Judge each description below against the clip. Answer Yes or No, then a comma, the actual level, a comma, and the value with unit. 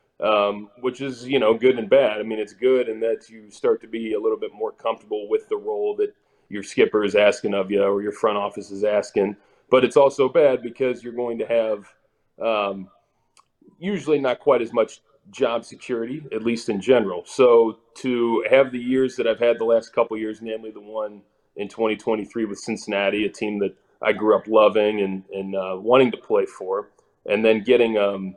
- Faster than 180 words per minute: Yes, fast, 205 wpm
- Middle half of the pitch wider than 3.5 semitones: Yes, average, 4.2 semitones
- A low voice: Yes, low, 115 Hz